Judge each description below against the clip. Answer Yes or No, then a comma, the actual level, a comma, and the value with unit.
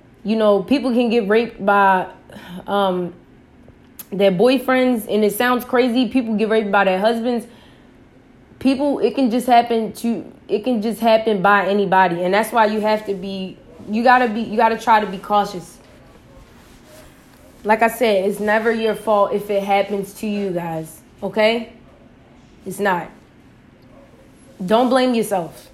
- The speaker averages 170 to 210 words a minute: No, average, 155 wpm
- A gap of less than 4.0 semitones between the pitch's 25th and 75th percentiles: Yes, average, 2.9 semitones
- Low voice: No, high, 215 Hz